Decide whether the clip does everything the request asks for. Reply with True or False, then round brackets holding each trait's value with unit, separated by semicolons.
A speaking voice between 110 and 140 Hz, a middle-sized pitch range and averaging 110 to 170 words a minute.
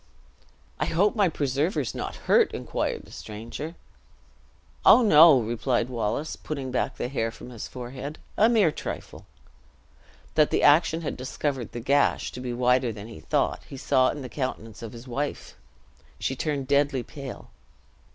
True (135 Hz; 3.7 semitones; 160 wpm)